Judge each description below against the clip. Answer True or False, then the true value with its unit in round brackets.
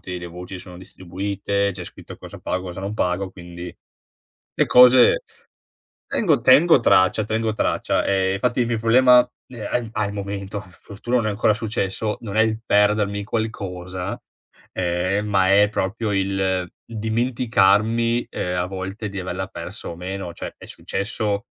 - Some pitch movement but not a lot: True (3.0 semitones)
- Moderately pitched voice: False (100 Hz)